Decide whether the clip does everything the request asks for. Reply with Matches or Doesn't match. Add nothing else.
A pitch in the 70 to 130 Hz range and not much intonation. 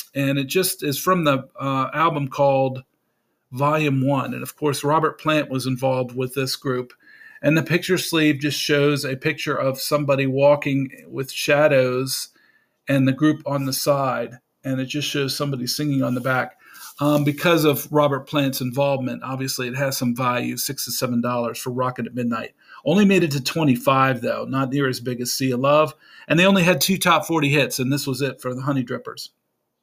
Doesn't match